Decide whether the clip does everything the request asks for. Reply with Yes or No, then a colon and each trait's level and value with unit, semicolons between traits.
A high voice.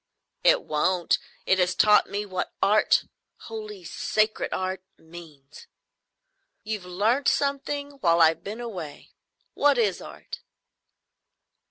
Yes: high, 195 Hz